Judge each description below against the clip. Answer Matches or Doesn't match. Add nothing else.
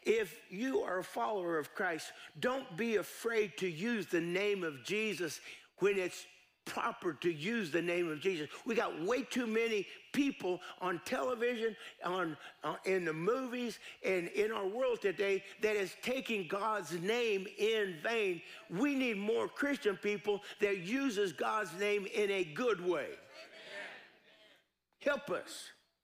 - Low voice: Doesn't match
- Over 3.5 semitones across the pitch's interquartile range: Matches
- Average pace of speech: Matches